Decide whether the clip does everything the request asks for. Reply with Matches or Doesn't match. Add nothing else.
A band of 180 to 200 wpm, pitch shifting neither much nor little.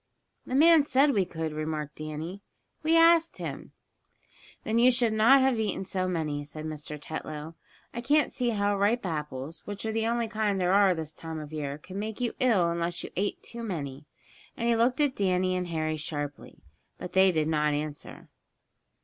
Doesn't match